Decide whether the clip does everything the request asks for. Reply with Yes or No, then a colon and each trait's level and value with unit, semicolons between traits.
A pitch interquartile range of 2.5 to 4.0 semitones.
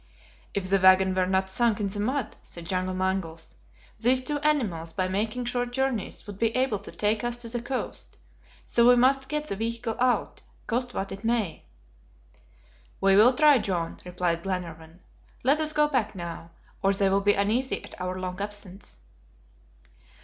No: average, 4.7 semitones